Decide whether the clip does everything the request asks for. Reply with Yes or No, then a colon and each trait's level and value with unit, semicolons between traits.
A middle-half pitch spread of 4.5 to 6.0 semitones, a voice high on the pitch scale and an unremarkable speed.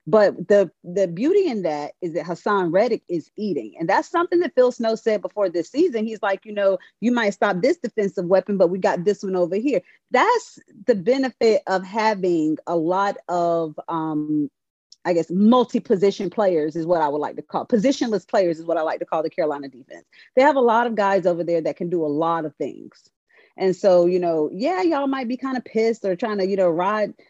No: average, 5.2 semitones; high, 200 Hz; fast, 225 wpm